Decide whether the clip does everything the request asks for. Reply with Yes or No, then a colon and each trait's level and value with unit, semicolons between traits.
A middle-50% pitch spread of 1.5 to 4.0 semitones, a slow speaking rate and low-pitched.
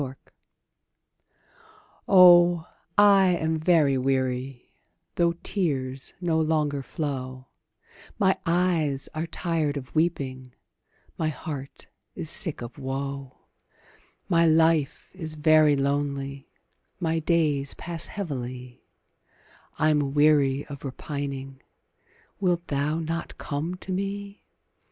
No: average, 3.5 semitones; slow, 100 wpm; medium, 150 Hz